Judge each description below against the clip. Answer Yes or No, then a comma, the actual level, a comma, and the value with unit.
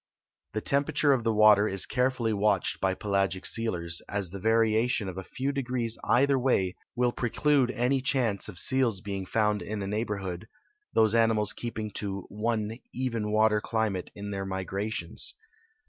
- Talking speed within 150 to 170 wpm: Yes, average, 160 wpm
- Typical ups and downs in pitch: Yes, average, 3.5 semitones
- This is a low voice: Yes, low, 110 Hz